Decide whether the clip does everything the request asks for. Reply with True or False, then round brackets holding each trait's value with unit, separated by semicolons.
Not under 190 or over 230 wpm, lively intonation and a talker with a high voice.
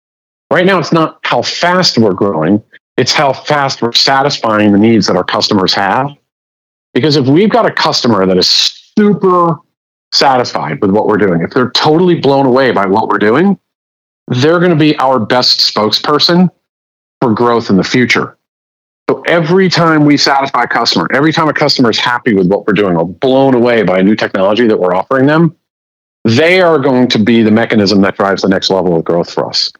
False (195 wpm; 7.9 semitones; 125 Hz)